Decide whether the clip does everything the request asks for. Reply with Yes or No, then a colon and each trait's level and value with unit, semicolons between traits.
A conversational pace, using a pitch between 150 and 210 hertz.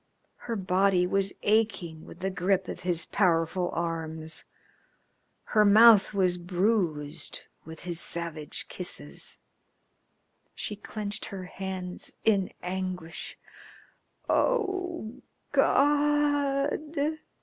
No: slow, 95 wpm; high, 190 Hz